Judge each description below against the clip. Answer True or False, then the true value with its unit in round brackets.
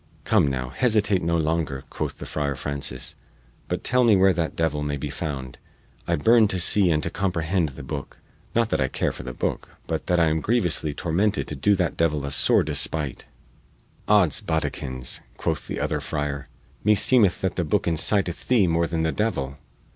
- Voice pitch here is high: False (80 Hz)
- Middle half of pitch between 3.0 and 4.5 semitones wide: False (5.2 semitones)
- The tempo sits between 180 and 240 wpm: True (190 wpm)